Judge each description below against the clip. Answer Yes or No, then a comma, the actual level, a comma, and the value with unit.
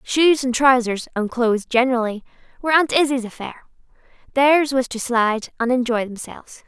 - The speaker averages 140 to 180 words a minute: Yes, average, 155 wpm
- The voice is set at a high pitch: Yes, very high, 250 Hz